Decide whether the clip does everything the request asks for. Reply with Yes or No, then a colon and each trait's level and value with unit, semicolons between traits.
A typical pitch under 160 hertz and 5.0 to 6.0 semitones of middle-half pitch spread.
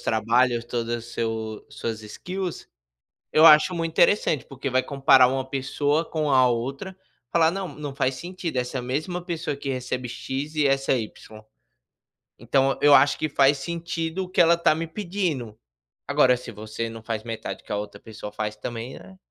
Yes: low, 135 Hz; wide, 5.5 semitones